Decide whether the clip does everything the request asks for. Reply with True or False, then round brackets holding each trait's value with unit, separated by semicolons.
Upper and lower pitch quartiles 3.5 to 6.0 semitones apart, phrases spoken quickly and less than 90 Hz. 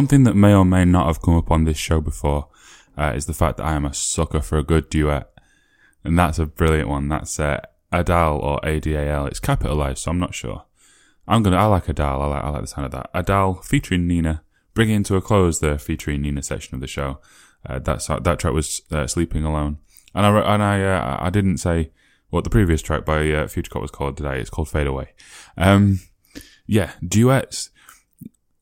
True (3.8 semitones; 220 wpm; 80 Hz)